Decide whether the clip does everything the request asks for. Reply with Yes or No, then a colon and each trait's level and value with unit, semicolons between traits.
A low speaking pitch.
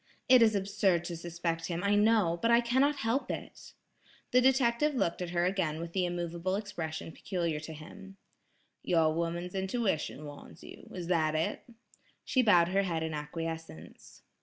No: medium, 175 Hz